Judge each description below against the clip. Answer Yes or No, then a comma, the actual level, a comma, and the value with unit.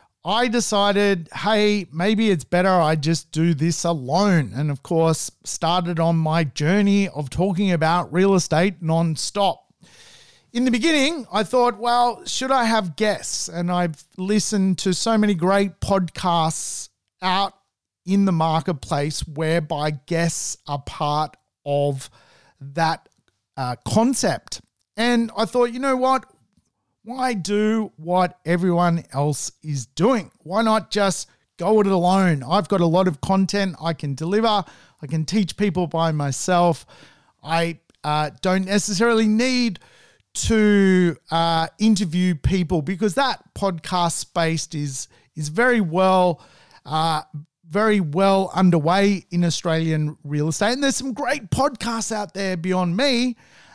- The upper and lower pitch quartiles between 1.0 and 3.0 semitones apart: No, average, 4.4 semitones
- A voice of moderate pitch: Yes, medium, 180 Hz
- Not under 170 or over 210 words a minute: No, slow, 135 wpm